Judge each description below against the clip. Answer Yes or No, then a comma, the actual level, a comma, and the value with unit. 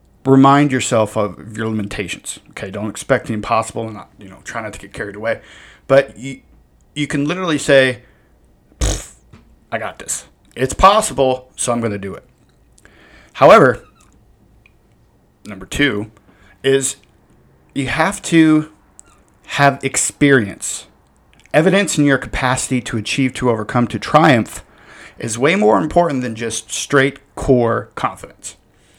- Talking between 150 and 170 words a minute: No, slow, 135 wpm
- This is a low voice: Yes, low, 125 Hz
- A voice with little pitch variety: No, average, 4.6 semitones